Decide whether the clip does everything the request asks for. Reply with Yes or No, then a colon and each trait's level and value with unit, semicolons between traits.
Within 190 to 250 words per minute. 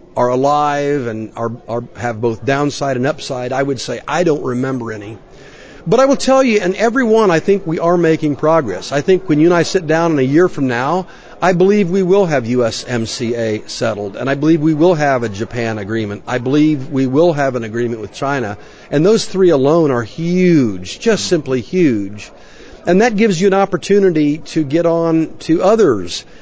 Yes: average, 200 wpm